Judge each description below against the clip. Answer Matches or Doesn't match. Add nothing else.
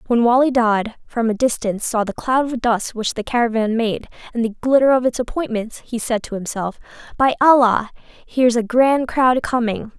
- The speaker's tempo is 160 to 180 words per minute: Doesn't match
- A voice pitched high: Matches